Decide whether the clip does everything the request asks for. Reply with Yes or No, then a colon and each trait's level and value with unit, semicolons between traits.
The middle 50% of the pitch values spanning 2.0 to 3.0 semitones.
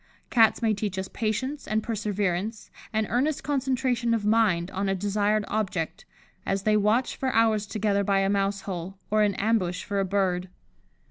Yes: narrow, 2.4 semitones